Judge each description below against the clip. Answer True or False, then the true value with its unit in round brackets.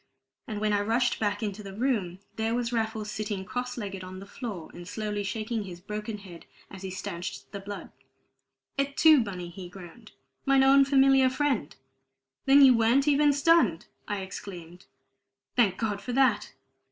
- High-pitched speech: True (215 Hz)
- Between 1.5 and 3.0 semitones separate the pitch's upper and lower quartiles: False (4.4 semitones)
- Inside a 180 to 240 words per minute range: False (170 wpm)